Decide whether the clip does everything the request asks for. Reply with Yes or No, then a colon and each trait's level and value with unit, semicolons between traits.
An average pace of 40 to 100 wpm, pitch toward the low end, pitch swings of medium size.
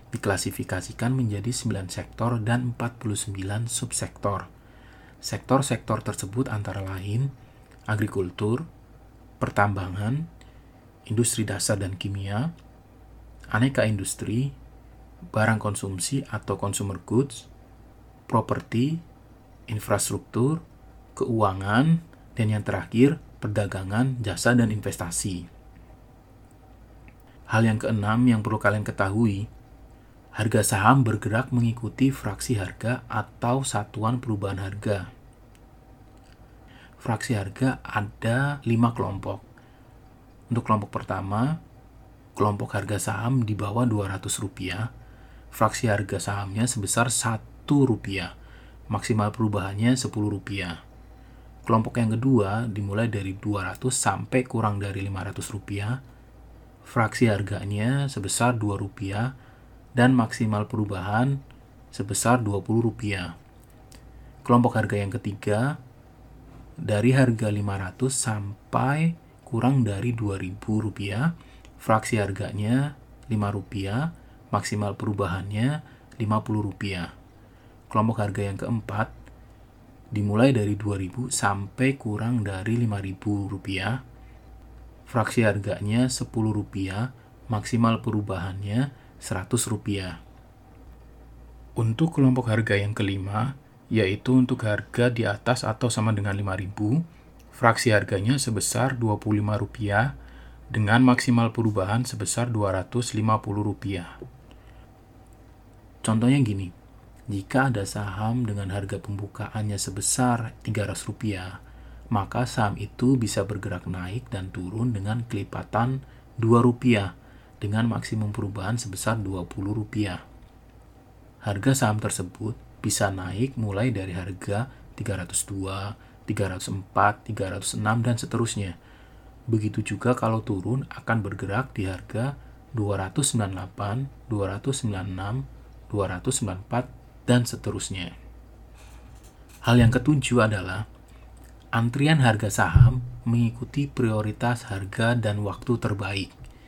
Yes: average, 90 wpm; low, 110 Hz; average, 3.4 semitones